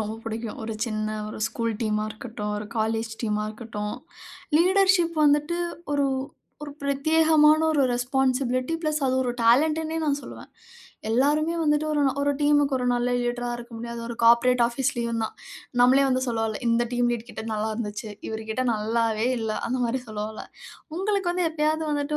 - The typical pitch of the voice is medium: No, high, 245 Hz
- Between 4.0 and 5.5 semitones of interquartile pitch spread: Yes, average, 4.9 semitones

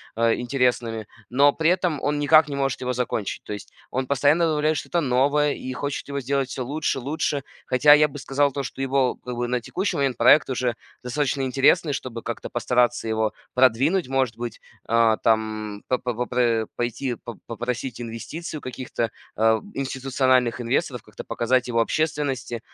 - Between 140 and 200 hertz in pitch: No, low, 130 Hz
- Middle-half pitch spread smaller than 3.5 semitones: Yes, average, 3.1 semitones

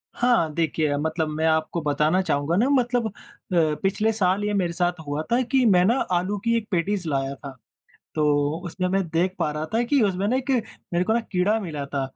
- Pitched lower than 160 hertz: No, medium, 180 Hz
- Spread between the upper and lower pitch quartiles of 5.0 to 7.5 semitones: Yes, average, 5.3 semitones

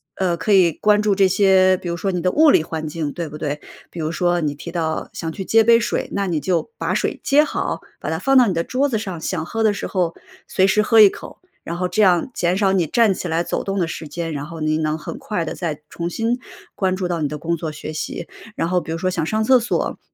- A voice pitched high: No, medium, 180 Hz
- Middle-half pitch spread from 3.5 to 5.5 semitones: Yes, average, 3.8 semitones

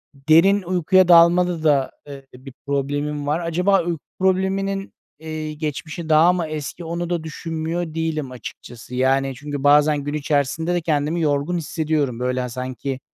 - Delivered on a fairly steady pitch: No, average, 3.3 semitones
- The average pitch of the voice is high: No, medium, 155 Hz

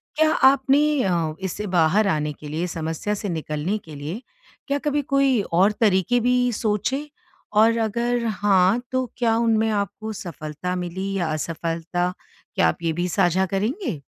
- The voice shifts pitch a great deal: Yes, wide, 5.8 semitones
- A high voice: Yes, high, 200 Hz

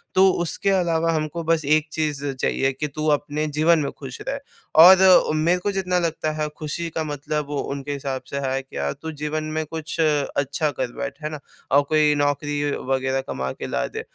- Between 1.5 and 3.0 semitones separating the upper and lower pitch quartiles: Yes, narrow, 2.4 semitones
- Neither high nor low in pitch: Yes, medium, 150 Hz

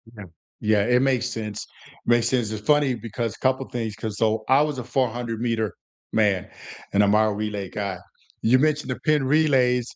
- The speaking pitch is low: Yes, low, 115 Hz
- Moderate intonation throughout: Yes, average, 3.3 semitones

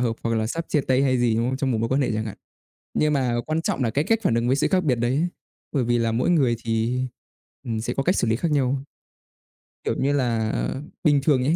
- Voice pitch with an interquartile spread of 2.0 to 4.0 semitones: Yes, average, 3.6 semitones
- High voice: No, low, 130 Hz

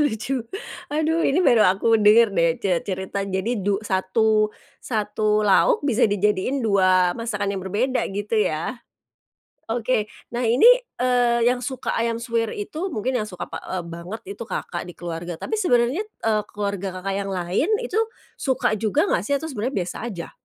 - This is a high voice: Yes, high, 215 Hz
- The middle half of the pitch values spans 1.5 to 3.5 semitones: No, average, 4.1 semitones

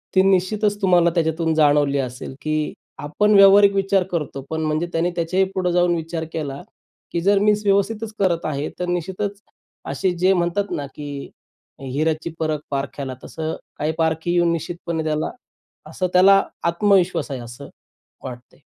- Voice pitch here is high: No, medium, 170 Hz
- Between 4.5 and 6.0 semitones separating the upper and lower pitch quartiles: No, average, 3.7 semitones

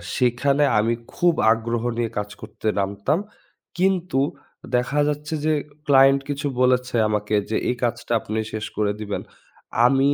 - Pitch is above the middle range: No, low, 125 Hz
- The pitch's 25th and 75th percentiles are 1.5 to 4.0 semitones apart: No, average, 4.6 semitones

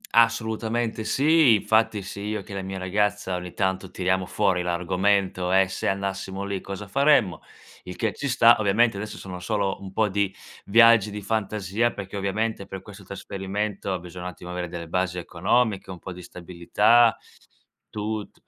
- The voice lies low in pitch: Yes, low, 100 Hz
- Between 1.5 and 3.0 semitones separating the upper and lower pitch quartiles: Yes, narrow, 2.6 semitones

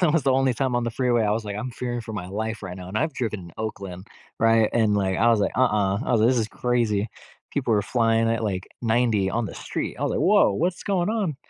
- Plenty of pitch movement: No, average, 3.3 semitones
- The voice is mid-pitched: No, low, 115 Hz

